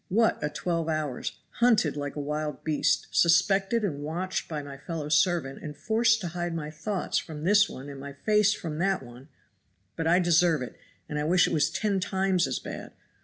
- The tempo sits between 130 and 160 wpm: No, average, 200 wpm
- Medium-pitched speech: Yes, medium, 165 Hz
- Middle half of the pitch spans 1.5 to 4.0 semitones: No, average, 4.4 semitones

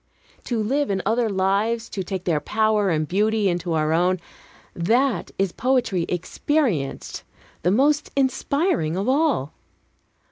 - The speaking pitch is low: No, high, 205 Hz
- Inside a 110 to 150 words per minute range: Yes, slow, 135 wpm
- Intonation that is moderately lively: No, wide, 5.9 semitones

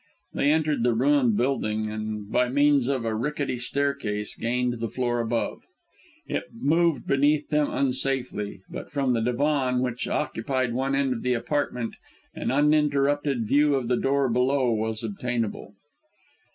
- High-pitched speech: No, low, 125 Hz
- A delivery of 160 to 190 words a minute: No, average, 150 wpm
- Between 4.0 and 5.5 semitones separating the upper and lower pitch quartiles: No, average, 3.5 semitones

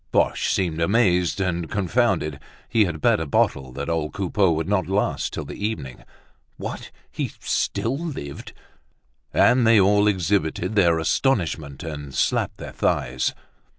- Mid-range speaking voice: No, very low, 90 Hz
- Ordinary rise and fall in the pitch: Yes, average, 4.7 semitones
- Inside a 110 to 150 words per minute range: Yes, average, 145 wpm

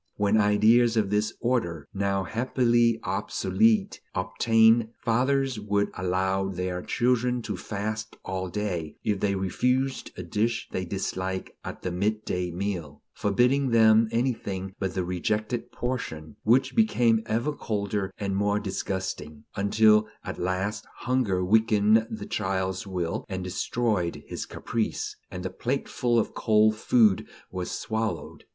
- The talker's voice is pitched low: Yes, low, 105 Hz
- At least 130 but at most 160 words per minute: Yes, slow, 135 wpm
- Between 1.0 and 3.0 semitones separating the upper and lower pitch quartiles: No, average, 3.5 semitones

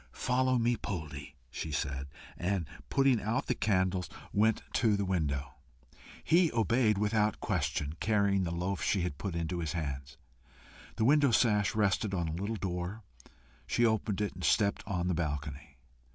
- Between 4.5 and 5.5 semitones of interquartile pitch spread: Yes, average, 4.9 semitones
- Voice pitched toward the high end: No, very low, 95 Hz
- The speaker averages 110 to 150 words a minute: No, average, 160 wpm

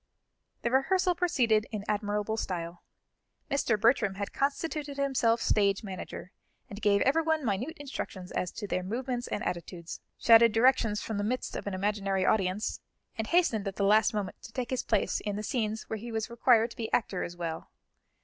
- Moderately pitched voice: No, high, 220 Hz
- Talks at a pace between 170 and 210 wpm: Yes, average, 180 wpm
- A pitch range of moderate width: Yes, average, 3.9 semitones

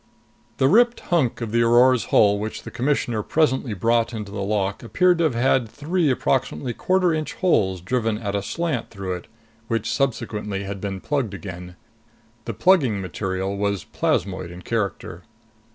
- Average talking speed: Yes, average, 165 wpm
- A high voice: No, low, 115 Hz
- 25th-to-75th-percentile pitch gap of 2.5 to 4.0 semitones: No, average, 5.1 semitones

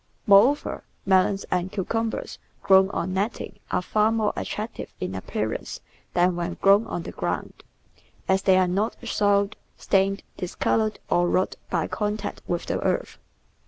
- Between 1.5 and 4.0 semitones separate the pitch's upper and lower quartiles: Yes, narrow, 2.6 semitones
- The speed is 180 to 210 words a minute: No, average, 145 wpm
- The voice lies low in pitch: No, high, 195 Hz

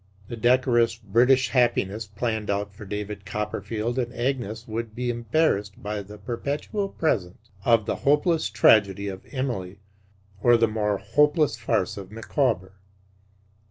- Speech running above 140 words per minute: No, slow, 135 wpm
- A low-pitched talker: Yes, low, 115 Hz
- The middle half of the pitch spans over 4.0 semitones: No, average, 3.3 semitones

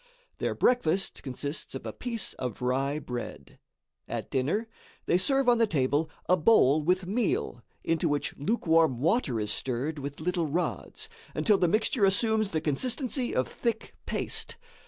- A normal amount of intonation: No, wide, 7.8 semitones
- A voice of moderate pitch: Yes, medium, 165 Hz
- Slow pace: No, average, 155 wpm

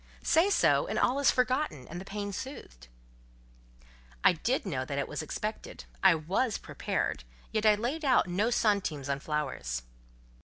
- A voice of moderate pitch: No, high, 200 Hz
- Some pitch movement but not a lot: No, wide, 8.6 semitones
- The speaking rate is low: No, average, 160 wpm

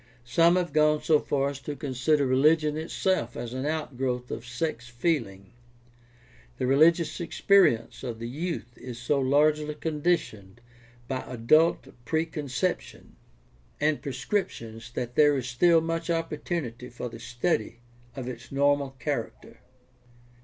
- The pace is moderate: No, slow, 130 wpm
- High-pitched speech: No, medium, 140 Hz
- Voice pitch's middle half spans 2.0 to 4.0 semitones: No, average, 4.5 semitones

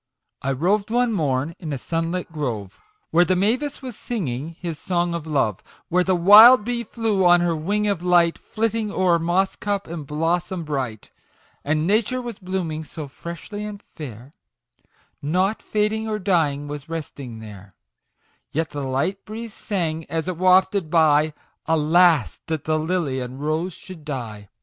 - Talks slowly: No, average, 165 wpm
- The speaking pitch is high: No, medium, 170 Hz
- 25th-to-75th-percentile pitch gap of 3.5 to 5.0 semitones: Yes, average, 4.7 semitones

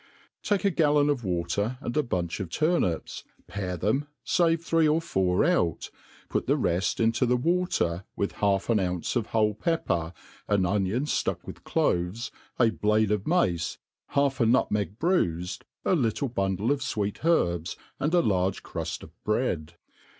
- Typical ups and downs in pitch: No, wide, 7.9 semitones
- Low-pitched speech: Yes, low, 110 Hz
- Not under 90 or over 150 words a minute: No, average, 165 wpm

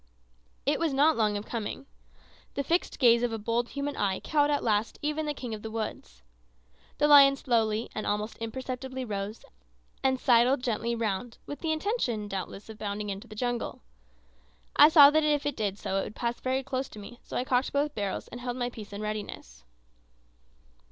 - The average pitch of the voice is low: No, high, 240 Hz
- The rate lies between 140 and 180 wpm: No, average, 195 wpm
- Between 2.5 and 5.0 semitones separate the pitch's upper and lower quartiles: Yes, average, 4.6 semitones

